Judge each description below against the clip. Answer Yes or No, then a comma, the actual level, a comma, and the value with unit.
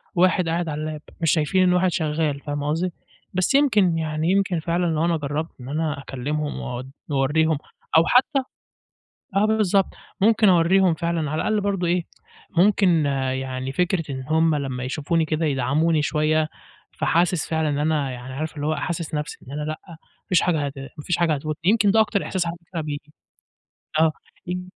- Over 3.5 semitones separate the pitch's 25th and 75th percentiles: No, average, 3.2 semitones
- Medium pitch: Yes, medium, 160 Hz